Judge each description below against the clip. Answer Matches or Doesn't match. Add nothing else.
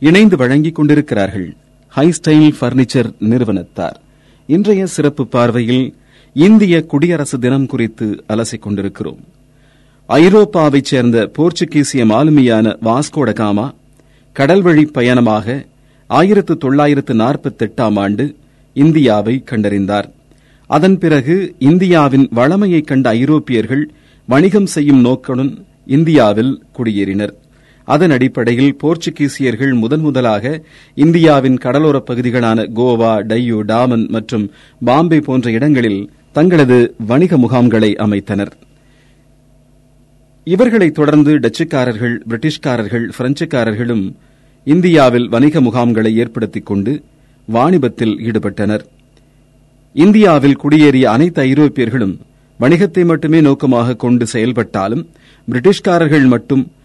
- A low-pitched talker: Matches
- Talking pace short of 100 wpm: Matches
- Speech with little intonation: Doesn't match